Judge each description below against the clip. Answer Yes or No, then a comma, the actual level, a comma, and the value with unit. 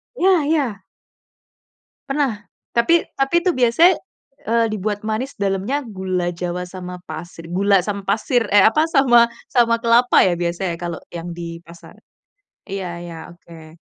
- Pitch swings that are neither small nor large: No, wide, 5.9 semitones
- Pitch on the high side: Yes, high, 200 Hz